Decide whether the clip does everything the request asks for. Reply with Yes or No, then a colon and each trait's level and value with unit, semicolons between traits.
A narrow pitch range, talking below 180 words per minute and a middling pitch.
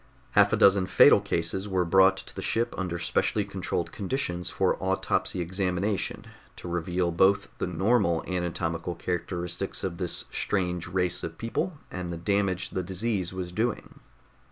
No: narrow, 2.0 semitones; average, 155 wpm; very low, 90 Hz